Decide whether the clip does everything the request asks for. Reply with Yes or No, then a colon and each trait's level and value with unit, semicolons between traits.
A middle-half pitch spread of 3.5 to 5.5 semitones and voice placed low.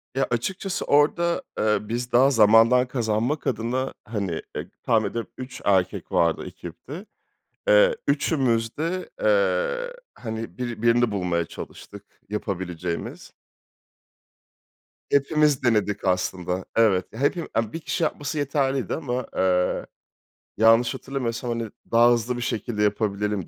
Yes: average, 5.0 semitones; low, 120 Hz